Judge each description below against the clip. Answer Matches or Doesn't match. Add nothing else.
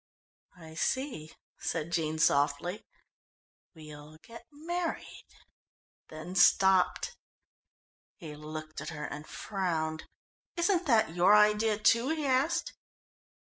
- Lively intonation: Matches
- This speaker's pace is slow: Matches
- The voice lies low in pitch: Doesn't match